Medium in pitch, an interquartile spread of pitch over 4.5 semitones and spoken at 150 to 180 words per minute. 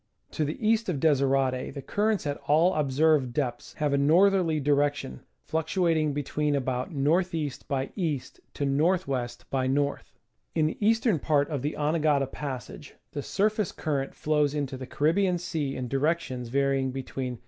No: medium, 145 Hz; average, 3.0 semitones; average, 165 wpm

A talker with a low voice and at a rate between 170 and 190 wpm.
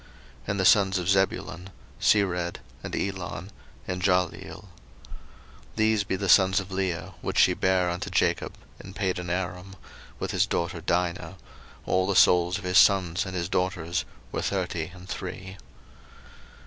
No: very low, 90 Hz; average, 150 wpm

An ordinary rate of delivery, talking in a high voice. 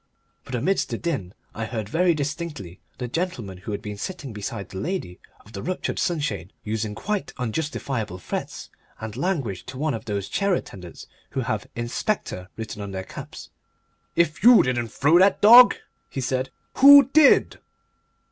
No: average, 165 wpm; low, 125 Hz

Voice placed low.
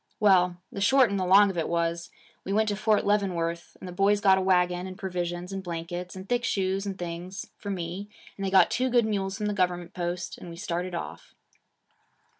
No: medium, 185 Hz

